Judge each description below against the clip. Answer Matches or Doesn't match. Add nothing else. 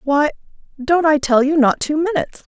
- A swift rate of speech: Doesn't match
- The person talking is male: Doesn't match